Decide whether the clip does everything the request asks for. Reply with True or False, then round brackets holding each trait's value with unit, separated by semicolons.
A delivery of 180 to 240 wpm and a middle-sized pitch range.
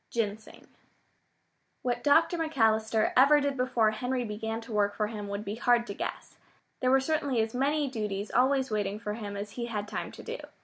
True (190 wpm; 3.9 semitones)